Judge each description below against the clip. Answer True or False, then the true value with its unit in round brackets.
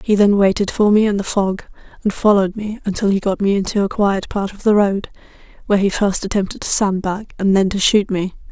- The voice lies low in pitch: False (200 Hz)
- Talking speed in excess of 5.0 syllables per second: True (5.8 syllables/s)